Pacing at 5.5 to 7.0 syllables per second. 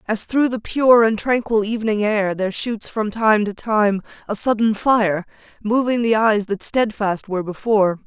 No: 4.7 syllables/s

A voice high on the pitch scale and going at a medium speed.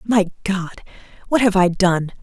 Yes: high, 195 Hz; average, 160 wpm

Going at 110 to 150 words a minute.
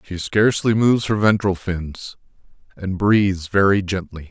Yes: average, 140 wpm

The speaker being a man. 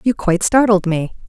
No: female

